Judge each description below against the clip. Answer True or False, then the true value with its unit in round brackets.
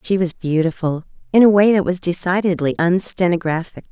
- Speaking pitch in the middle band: True (180 Hz)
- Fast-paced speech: False (155 wpm)